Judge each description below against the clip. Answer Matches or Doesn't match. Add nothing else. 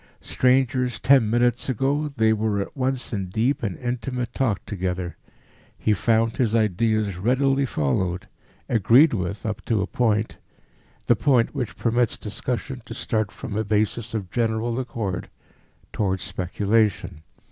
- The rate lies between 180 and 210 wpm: Doesn't match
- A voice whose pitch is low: Matches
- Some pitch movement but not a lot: Matches